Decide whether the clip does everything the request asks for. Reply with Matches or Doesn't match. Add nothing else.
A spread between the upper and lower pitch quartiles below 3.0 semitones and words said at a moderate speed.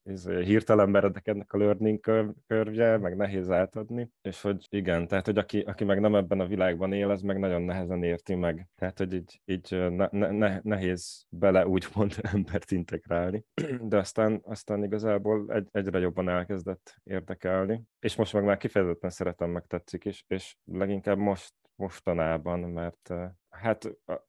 Doesn't match